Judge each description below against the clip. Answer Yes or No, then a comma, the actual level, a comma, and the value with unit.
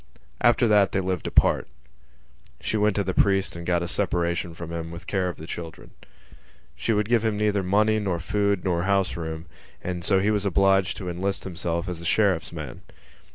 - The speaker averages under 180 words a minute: No, average, 200 wpm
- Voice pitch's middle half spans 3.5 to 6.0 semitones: No, average, 3.0 semitones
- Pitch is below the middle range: Yes, very low, 95 Hz